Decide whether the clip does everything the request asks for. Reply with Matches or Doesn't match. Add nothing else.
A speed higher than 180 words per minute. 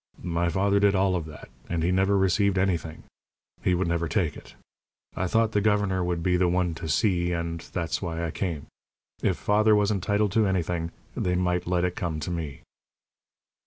Matches